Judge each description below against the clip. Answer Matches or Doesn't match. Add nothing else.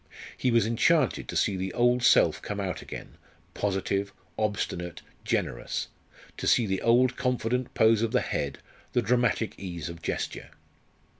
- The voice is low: Matches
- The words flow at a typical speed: Matches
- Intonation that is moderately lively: Matches